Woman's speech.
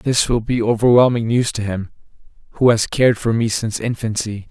No: male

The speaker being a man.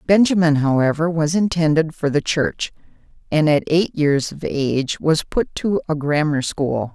No: female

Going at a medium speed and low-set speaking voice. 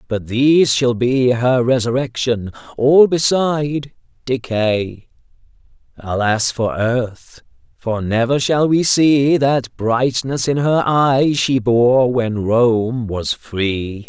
No: slow, 115 wpm; low, 125 Hz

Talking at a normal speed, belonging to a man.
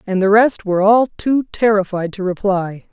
No: average, 185 wpm; female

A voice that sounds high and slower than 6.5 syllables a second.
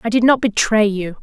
Yes: high, 220 Hz; 5.5 syllables/s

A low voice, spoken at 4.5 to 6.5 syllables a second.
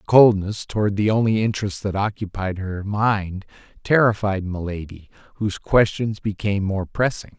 Yes: low, 100 Hz; 5.0 syllables/s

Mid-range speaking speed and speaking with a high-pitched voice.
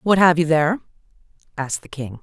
No: average, 190 wpm; medium, 160 Hz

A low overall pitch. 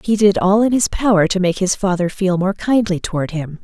No: high, 190 Hz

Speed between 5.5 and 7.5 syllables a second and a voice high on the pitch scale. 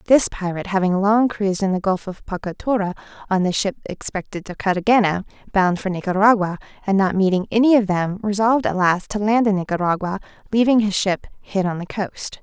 Yes: 5.8 syllables/s; high, 195 Hz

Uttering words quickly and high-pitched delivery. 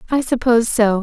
No: average, 175 wpm; high, 235 Hz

